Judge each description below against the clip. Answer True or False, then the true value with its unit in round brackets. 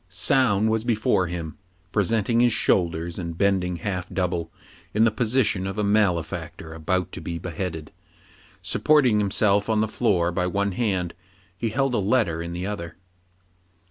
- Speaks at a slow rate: False (160 wpm)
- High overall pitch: False (95 Hz)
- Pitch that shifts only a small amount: False (4.1 semitones)